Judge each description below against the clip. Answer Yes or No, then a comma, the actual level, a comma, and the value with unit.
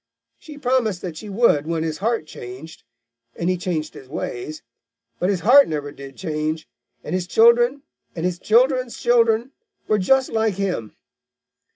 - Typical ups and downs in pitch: No, wide, 7.1 semitones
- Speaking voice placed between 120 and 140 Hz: No, medium, 185 Hz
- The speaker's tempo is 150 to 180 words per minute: Yes, average, 160 wpm